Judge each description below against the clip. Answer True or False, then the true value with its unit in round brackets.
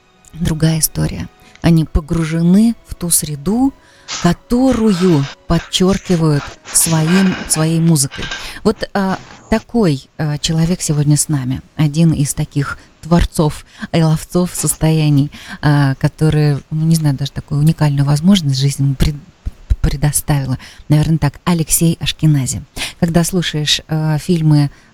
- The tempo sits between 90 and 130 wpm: True (110 wpm)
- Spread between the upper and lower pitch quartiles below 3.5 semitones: True (3.0 semitones)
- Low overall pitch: False (155 Hz)